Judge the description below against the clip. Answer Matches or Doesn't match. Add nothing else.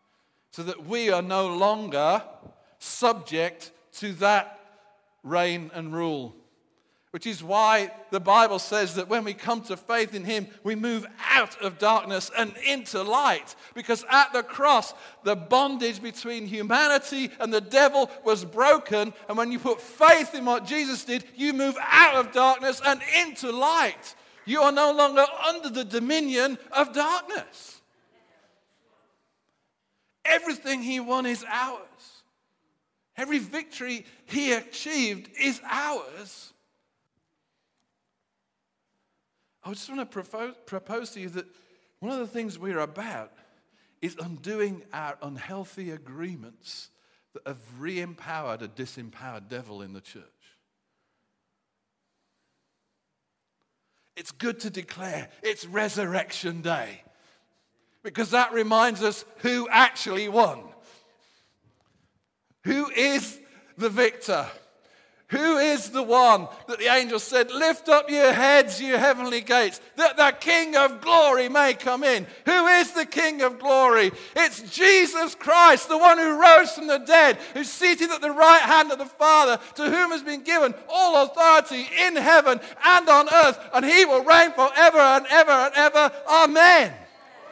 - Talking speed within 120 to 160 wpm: Matches